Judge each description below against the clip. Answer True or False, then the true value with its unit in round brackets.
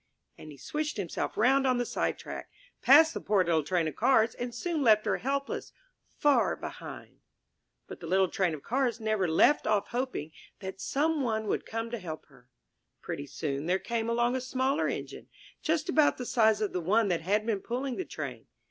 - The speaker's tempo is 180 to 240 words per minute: True (200 wpm)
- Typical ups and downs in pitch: False (6.0 semitones)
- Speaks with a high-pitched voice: True (225 Hz)